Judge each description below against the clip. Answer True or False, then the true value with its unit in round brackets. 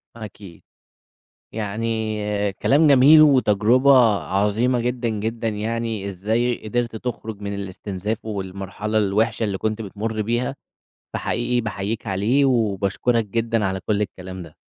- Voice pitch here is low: True (110 Hz)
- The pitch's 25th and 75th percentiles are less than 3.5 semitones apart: True (2.8 semitones)